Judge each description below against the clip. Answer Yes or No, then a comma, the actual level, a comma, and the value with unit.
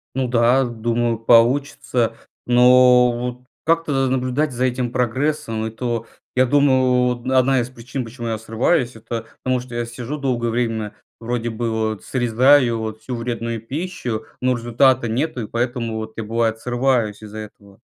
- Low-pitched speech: Yes, low, 120 Hz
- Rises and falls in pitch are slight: Yes, narrow, 2.1 semitones